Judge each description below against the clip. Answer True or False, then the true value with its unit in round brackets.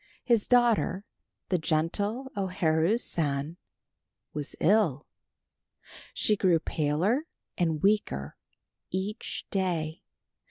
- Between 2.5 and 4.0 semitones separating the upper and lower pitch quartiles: False (5.0 semitones)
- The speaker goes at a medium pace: False (90 wpm)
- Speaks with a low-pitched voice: False (180 Hz)